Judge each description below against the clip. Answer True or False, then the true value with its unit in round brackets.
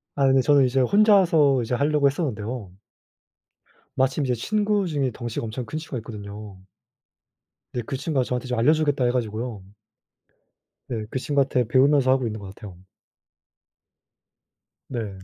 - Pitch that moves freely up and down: False (3.9 semitones)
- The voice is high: False (130 Hz)